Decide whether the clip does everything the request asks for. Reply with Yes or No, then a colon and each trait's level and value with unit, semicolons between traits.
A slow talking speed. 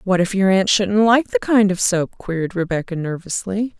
No: fast, 205 wpm